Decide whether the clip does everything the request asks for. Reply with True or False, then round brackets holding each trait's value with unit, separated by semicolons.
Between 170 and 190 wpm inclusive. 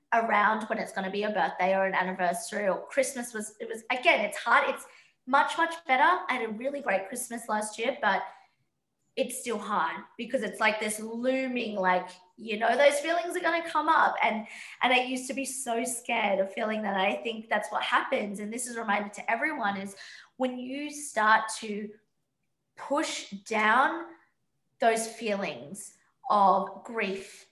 True (185 wpm)